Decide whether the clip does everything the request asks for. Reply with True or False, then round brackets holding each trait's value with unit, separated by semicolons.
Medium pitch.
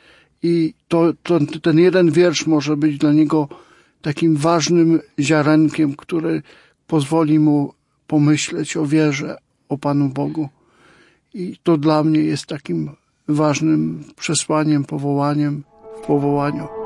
True (155 Hz)